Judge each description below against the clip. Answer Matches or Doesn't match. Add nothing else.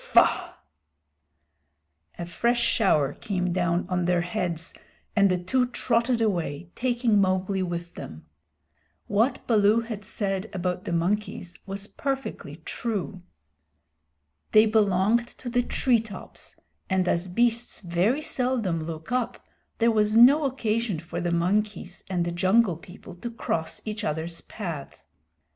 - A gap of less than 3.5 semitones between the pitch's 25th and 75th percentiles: Doesn't match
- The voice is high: Matches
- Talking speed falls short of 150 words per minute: Matches